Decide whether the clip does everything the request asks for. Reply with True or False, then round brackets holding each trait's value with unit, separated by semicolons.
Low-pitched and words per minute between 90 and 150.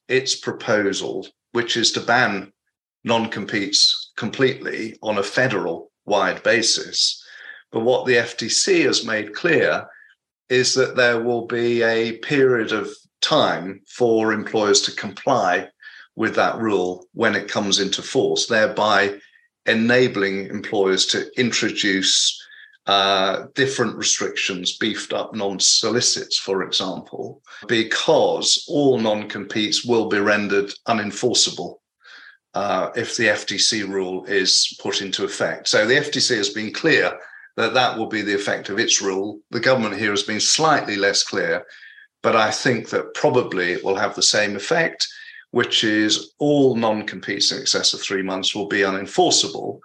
True (105 Hz; 145 wpm)